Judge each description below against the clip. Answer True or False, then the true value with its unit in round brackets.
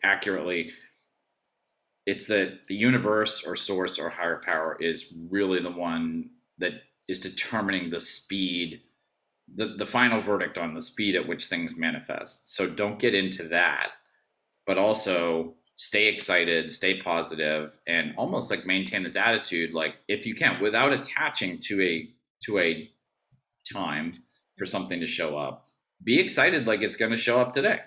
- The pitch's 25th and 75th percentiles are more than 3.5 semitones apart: True (4.5 semitones)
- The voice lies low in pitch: True (90 Hz)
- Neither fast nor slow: True (155 wpm)